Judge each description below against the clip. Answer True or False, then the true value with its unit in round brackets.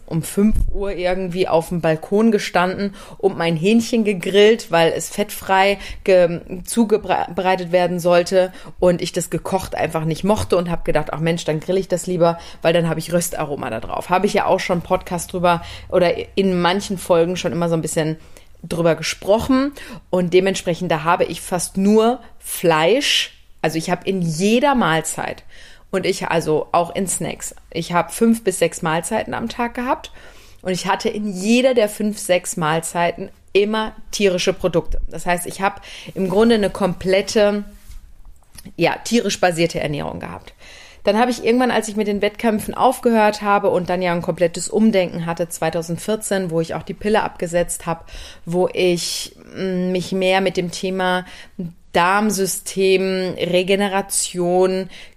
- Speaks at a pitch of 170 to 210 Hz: True (185 Hz)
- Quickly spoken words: False (165 wpm)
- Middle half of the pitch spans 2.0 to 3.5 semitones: True (2.9 semitones)